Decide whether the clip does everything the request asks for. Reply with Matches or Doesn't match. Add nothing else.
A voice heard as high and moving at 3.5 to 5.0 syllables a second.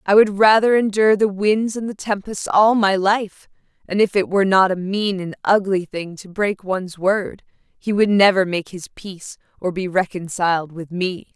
Matches